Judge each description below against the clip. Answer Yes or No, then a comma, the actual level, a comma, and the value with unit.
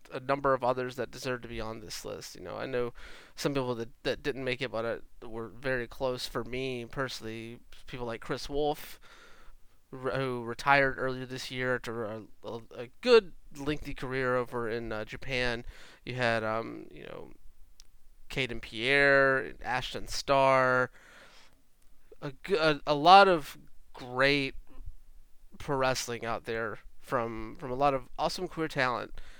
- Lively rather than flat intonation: No, average, 2.8 semitones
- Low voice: Yes, low, 130 Hz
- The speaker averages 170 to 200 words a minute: No, average, 155 wpm